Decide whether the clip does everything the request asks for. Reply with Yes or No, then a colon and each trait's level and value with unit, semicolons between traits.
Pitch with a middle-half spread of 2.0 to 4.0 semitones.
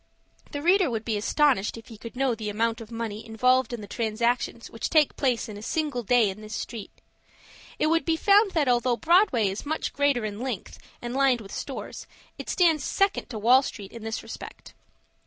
No: average, 4.5 semitones